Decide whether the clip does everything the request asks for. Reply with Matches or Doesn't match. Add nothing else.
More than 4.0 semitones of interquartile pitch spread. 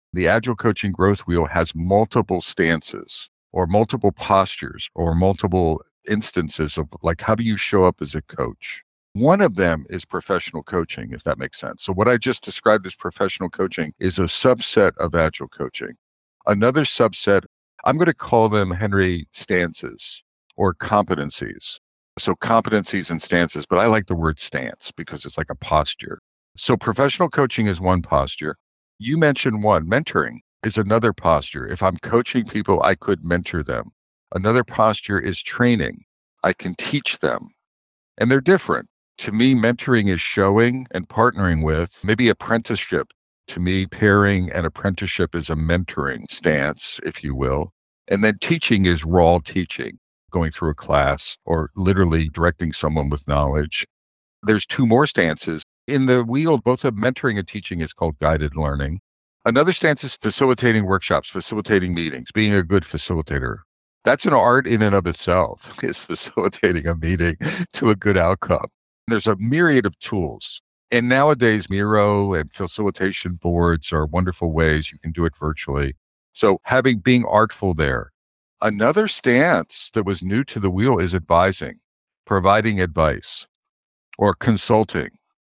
Matches